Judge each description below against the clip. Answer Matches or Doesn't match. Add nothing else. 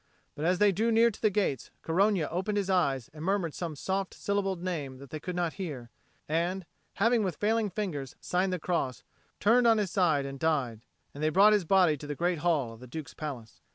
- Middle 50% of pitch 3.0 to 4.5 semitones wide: Doesn't match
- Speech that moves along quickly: Matches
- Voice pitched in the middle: Matches